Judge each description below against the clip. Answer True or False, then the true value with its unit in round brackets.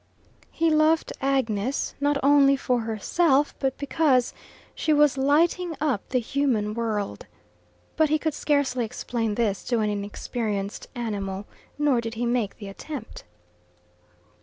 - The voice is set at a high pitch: True (255 Hz)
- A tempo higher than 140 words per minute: False (135 wpm)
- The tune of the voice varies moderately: True (4.8 semitones)